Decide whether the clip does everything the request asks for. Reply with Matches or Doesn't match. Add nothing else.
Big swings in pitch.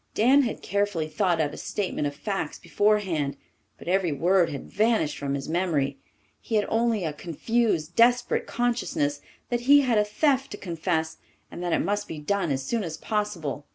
Matches